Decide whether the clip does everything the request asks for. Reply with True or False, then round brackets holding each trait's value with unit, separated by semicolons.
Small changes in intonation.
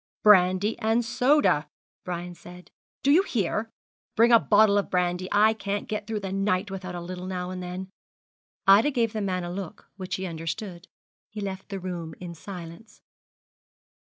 False (3.1 semitones)